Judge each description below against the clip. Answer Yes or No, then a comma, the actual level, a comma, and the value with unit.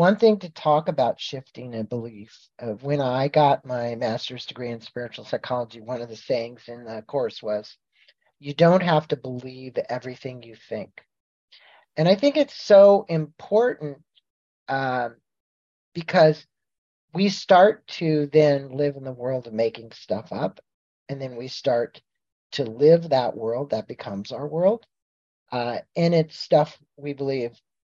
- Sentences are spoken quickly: No, average, 155 wpm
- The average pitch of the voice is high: No, low, 135 Hz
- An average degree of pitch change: Yes, average, 4.7 semitones